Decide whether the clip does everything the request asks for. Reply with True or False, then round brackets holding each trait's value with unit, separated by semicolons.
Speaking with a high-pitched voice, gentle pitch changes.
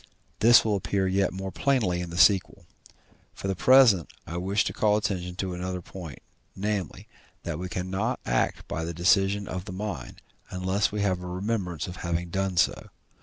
False (95 Hz; 2.3 semitones)